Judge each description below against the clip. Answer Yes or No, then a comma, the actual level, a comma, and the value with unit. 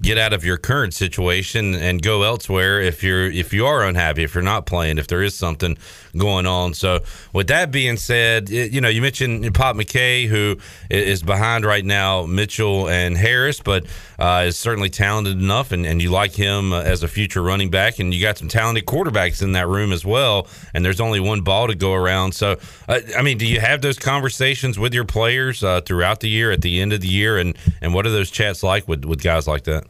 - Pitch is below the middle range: Yes, low, 100 Hz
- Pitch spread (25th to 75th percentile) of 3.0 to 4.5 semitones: Yes, average, 3.7 semitones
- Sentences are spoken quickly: Yes, fast, 230 wpm